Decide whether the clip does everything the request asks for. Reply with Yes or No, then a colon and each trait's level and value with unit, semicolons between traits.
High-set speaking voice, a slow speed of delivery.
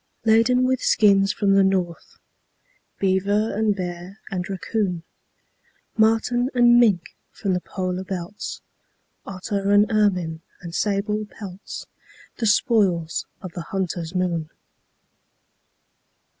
Yes: high, 195 Hz; slow, 110 wpm